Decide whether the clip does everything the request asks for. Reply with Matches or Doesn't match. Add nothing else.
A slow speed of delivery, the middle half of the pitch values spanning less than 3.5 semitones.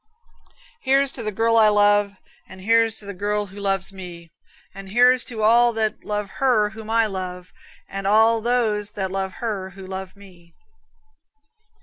Doesn't match